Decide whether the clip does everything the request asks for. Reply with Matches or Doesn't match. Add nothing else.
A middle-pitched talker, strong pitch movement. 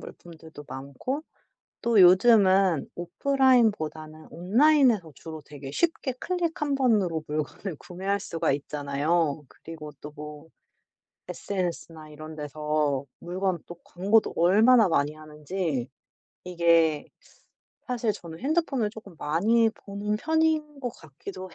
Matches